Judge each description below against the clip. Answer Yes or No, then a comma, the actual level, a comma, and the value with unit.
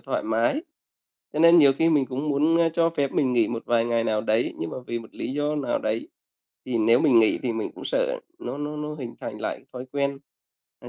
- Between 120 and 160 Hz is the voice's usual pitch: Yes, low, 135 Hz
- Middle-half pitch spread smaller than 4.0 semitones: No, average, 4.5 semitones